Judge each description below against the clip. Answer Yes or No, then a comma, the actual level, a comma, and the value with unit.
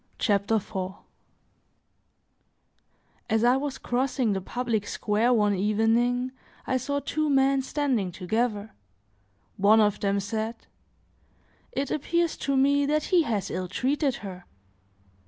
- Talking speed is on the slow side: Yes, slow, 120 wpm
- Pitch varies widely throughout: No, average, 4.8 semitones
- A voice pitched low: No, high, 235 Hz